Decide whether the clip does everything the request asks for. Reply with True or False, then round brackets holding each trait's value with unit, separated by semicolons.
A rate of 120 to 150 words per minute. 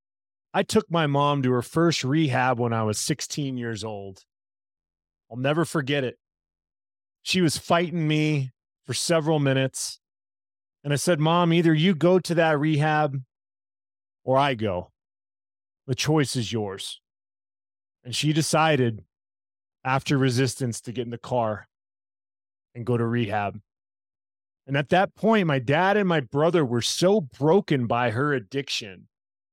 True (145 wpm)